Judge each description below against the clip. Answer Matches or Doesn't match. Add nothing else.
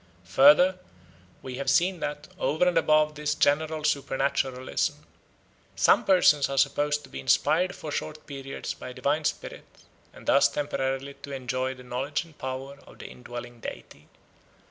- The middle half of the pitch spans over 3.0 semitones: Doesn't match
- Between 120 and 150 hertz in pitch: Matches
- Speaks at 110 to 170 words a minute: Matches